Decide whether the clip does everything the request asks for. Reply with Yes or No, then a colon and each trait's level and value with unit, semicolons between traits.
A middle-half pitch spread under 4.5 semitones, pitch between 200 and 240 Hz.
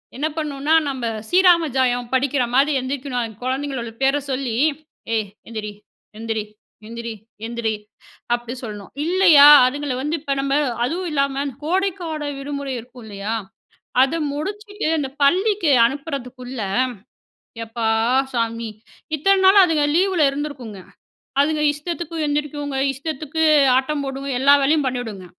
No: average, 4.1 semitones; very high, 275 Hz